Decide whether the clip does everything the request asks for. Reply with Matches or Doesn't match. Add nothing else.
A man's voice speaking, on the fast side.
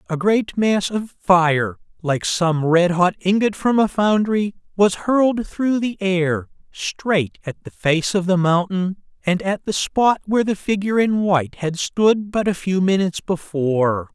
Doesn't match